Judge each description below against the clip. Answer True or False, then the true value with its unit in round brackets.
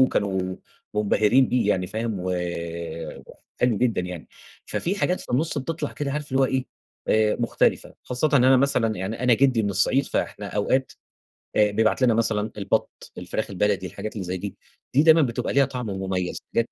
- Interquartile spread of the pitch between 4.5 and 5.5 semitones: True (4.8 semitones)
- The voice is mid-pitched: False (115 Hz)